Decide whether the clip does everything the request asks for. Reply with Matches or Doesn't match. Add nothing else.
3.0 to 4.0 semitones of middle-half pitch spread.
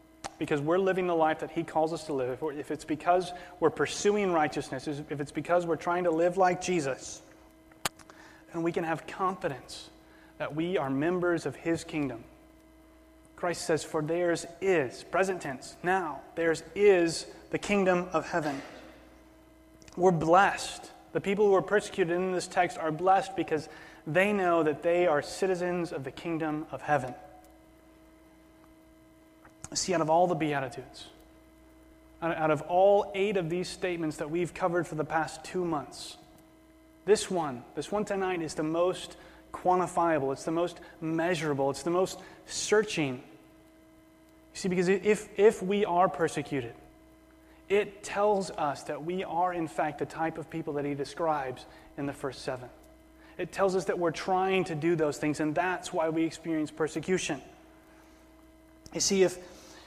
Matches